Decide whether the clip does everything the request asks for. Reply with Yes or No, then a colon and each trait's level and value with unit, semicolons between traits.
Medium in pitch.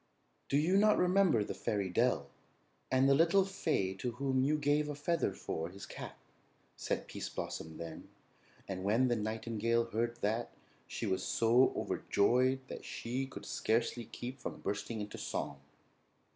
No: low, 120 Hz